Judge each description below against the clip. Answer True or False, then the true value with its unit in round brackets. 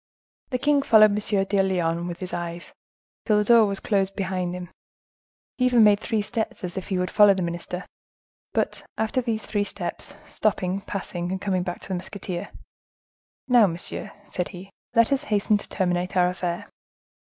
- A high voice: True (195 Hz)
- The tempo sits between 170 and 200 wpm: True (180 wpm)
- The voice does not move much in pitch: False (3.0 semitones)